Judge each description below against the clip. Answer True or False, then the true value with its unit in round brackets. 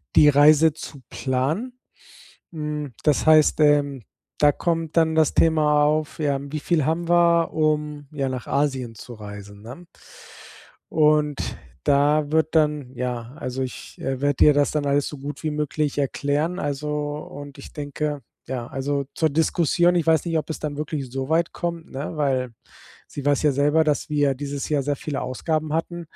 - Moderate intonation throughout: False (2.1 semitones)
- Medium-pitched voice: True (150 Hz)